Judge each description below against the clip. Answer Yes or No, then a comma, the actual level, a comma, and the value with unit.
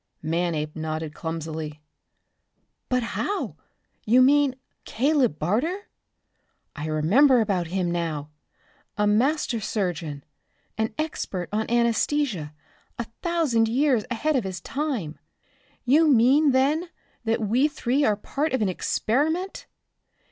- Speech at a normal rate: No, slow, 115 wpm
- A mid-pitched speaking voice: No, high, 225 Hz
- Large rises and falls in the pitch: Yes, wide, 8.6 semitones